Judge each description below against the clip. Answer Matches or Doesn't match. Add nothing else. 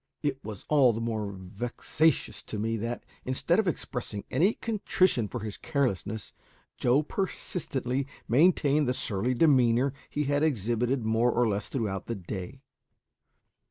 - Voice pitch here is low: Matches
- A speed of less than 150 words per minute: Matches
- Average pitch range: Matches